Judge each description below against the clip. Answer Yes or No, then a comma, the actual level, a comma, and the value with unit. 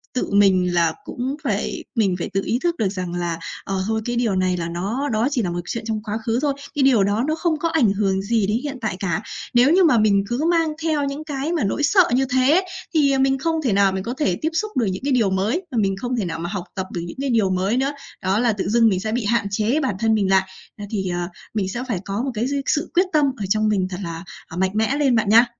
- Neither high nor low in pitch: No, high, 220 Hz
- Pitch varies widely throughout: Yes, wide, 5.8 semitones